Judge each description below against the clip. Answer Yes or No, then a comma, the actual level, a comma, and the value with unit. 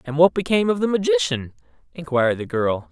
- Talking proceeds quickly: No, average, 185 wpm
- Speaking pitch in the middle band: Yes, medium, 150 Hz